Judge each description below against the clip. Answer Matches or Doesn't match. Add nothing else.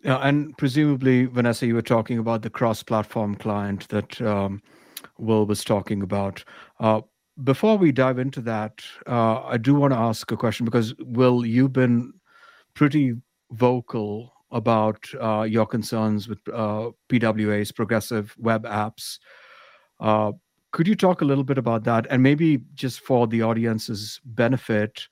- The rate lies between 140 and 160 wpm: Matches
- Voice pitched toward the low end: Matches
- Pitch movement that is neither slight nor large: Matches